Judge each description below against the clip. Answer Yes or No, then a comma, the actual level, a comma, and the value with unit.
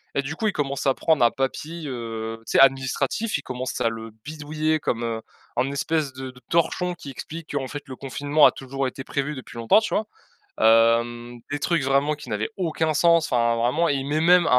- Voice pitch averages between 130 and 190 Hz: Yes, medium, 140 Hz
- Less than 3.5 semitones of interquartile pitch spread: No, average, 4.1 semitones